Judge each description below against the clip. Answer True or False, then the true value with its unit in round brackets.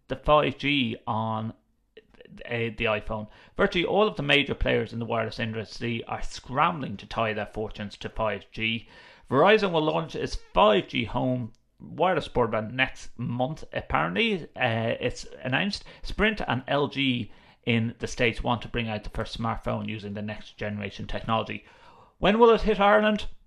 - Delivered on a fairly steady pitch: False (4.4 semitones)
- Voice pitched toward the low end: True (115 Hz)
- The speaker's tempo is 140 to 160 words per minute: True (155 wpm)